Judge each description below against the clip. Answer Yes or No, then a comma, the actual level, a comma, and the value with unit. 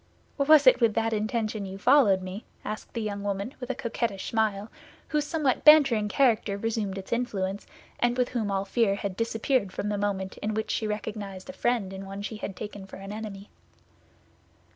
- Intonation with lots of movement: No, average, 3.0 semitones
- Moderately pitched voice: No, high, 215 Hz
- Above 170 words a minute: Yes, average, 190 wpm